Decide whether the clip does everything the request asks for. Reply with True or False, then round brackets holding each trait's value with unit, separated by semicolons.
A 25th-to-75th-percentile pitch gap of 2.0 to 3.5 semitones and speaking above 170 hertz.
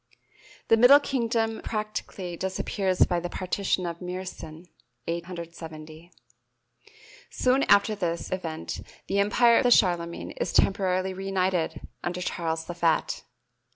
True (3.2 semitones; 185 Hz)